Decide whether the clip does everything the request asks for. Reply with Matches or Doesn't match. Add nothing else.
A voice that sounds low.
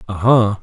Matches